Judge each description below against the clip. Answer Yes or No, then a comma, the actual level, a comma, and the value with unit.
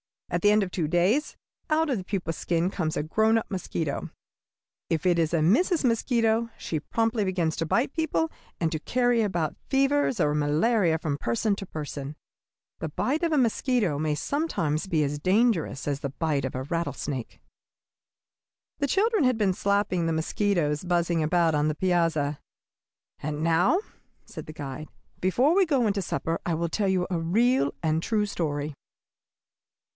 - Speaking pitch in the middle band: Yes, medium, 175 Hz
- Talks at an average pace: Yes, average, 175 wpm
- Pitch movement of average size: No, wide, 6.5 semitones